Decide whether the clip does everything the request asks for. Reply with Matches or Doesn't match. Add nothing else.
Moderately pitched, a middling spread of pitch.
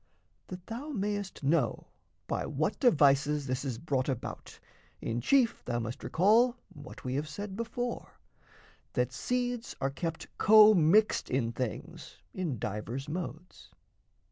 Doesn't match